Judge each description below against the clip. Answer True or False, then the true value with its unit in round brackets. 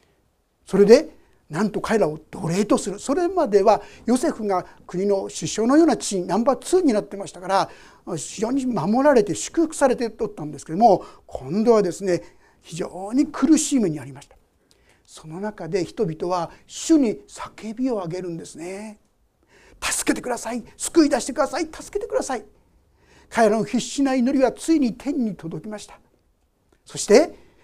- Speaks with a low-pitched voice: False (220 Hz)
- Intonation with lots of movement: True (6.8 semitones)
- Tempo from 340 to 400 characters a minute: False (330 characters per minute)